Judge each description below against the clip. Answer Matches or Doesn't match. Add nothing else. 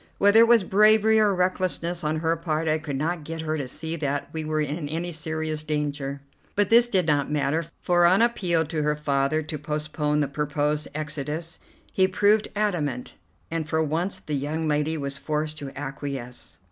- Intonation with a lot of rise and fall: Doesn't match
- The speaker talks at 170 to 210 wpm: Matches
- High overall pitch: Doesn't match